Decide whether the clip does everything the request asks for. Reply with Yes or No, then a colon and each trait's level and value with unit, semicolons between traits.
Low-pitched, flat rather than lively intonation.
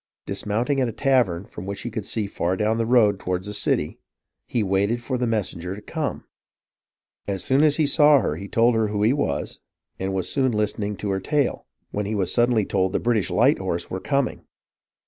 No: low, 105 Hz; average, 4.0 semitones